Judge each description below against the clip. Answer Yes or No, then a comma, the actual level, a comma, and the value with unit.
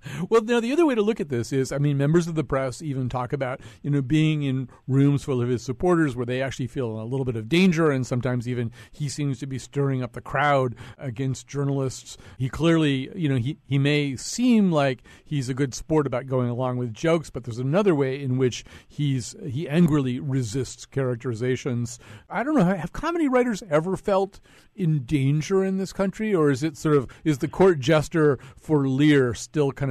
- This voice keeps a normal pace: No, fast, 210 wpm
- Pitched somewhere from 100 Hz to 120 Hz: No, medium, 140 Hz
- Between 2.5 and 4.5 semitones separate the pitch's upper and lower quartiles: Yes, average, 3.7 semitones